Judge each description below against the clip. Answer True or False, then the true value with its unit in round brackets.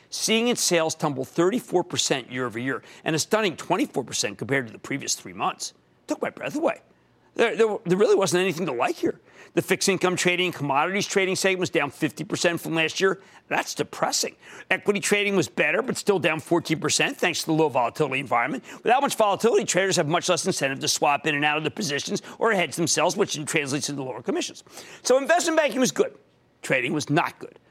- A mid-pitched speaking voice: True (175 Hz)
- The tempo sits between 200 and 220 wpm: True (205 wpm)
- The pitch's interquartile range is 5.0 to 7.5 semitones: False (4.5 semitones)